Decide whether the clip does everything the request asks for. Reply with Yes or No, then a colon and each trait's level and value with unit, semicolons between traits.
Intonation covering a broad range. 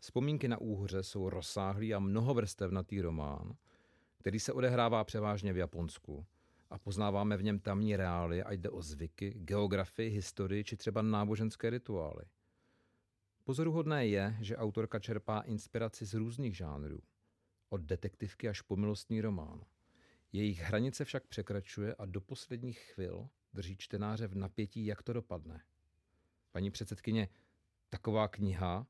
No: average, 2.7 semitones